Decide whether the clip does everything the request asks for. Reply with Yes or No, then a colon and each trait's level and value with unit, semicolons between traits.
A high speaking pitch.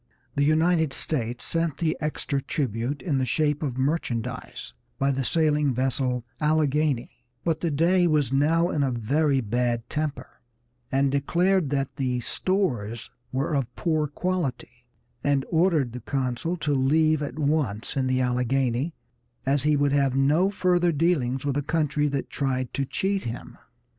No: medium, 140 Hz